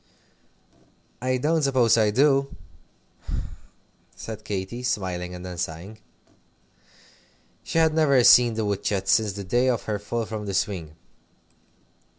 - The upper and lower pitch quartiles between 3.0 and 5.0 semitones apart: Yes, average, 4.7 semitones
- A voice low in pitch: Yes, low, 110 Hz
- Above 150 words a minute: No, slow, 135 wpm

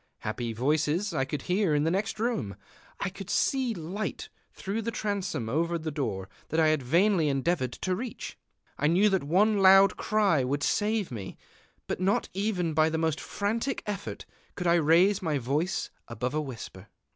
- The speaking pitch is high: No, medium, 170 Hz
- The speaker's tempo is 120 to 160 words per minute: No, average, 180 wpm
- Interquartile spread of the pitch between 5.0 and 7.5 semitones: Yes, wide, 5.5 semitones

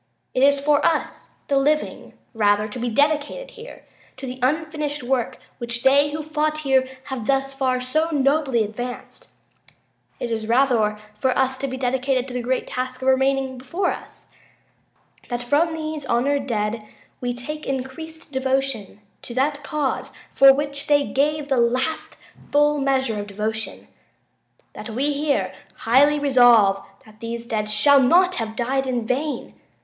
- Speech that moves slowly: No, average, 155 wpm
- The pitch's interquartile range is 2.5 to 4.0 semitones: Yes, average, 3.2 semitones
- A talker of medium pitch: No, very high, 265 Hz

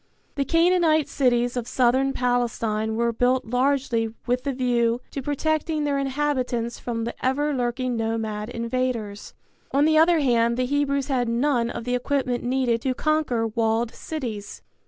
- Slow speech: No, average, 155 wpm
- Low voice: No, very high, 250 Hz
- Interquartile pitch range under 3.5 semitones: Yes, average, 3.1 semitones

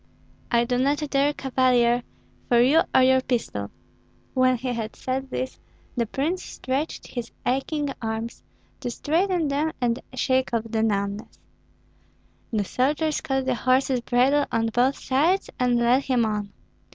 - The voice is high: Yes, very high, 255 Hz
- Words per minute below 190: Yes, average, 150 wpm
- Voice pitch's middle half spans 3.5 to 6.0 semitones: No, average, 2.7 semitones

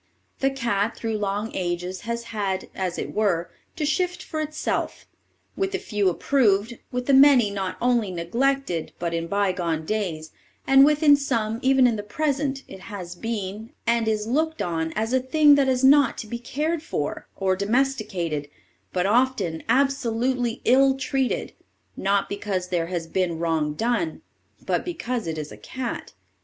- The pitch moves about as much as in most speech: No, wide, 6.3 semitones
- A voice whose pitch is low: No, high, 225 Hz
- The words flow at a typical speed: Yes, average, 165 wpm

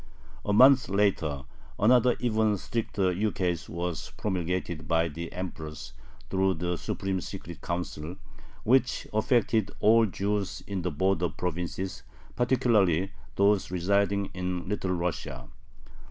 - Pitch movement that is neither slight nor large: Yes, average, 3.3 semitones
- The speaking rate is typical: No, slow, 115 wpm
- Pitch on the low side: Yes, very low, 95 Hz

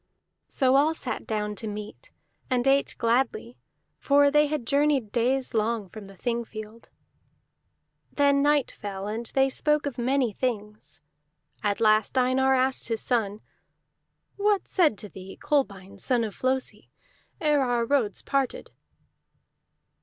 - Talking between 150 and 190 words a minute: No, average, 140 wpm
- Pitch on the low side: No, high, 245 Hz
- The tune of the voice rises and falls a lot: No, average, 4.5 semitones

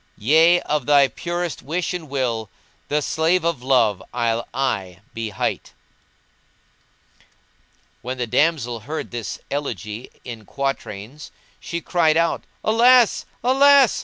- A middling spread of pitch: No, wide, 6.3 semitones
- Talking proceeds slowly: Yes, slow, 125 wpm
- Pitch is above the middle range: No, medium, 140 Hz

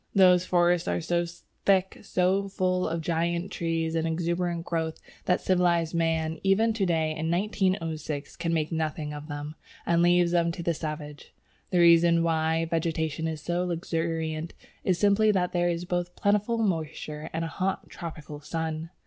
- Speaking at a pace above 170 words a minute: No, average, 165 wpm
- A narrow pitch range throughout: Yes, narrow, 1.8 semitones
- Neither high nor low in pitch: Yes, medium, 170 Hz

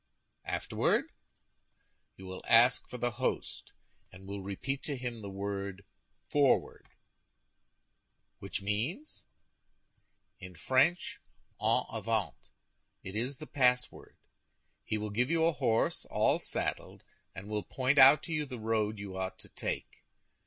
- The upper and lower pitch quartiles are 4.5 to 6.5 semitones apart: Yes, average, 4.9 semitones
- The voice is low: Yes, low, 115 Hz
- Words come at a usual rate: No, slow, 130 wpm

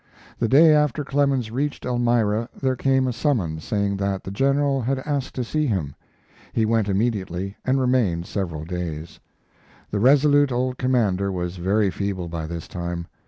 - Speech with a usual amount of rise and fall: No, wide, 6.1 semitones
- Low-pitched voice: Yes, low, 110 Hz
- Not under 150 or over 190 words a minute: Yes, average, 165 wpm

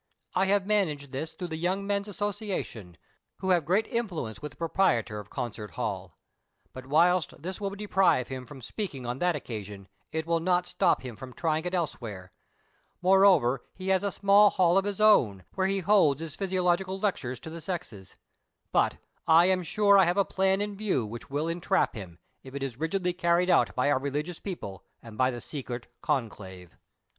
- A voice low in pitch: No, medium, 165 Hz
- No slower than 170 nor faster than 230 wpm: Yes, average, 190 wpm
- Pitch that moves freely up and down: Yes, wide, 6.9 semitones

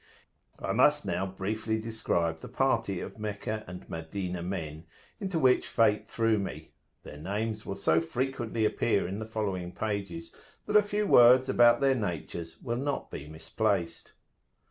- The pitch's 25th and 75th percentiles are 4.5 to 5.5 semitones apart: Yes, average, 5.0 semitones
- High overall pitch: No, low, 105 Hz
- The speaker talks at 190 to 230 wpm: No, average, 155 wpm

